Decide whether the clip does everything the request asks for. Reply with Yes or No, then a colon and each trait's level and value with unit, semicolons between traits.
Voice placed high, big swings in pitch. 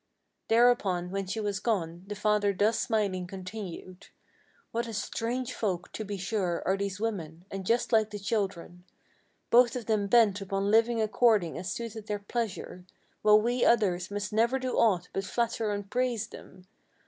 No: high, 205 Hz; average, 3.2 semitones